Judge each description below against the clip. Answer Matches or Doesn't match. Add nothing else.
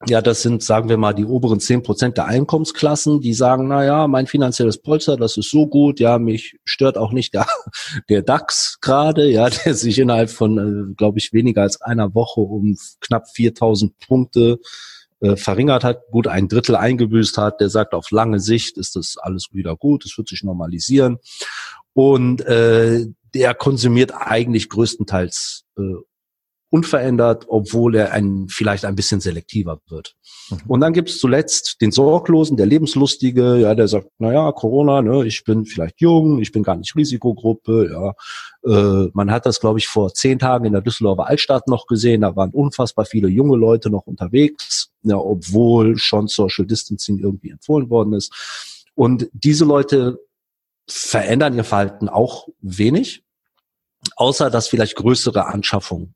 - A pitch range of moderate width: Matches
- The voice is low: Matches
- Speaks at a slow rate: Doesn't match